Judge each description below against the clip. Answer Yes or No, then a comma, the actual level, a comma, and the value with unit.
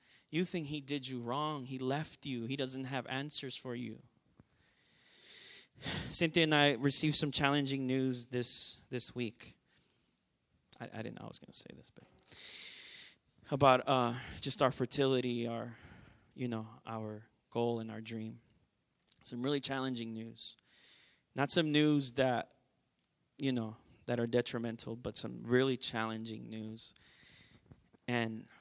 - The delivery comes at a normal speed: Yes, average, 145 wpm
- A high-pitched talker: No, low, 125 Hz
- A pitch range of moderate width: Yes, average, 3.0 semitones